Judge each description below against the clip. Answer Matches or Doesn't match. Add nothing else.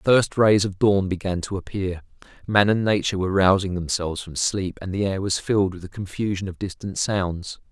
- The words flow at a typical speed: Doesn't match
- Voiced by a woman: Doesn't match